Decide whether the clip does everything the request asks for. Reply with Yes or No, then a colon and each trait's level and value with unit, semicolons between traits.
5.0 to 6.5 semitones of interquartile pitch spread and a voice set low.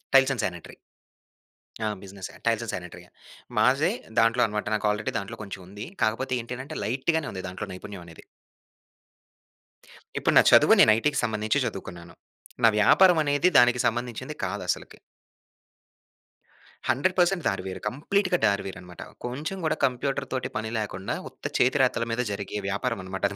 Yes: average, 5.3 semitones; low, 115 Hz